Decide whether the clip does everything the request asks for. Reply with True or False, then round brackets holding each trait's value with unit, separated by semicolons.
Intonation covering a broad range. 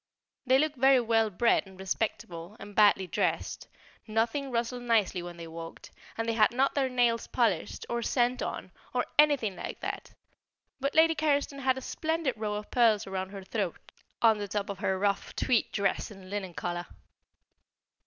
False (4.7 semitones)